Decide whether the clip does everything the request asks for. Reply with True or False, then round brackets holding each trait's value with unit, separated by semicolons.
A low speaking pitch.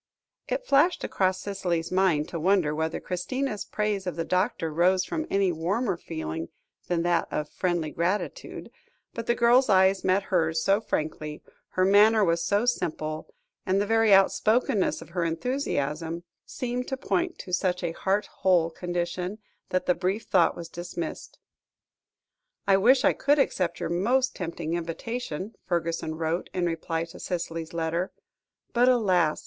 False (185 Hz)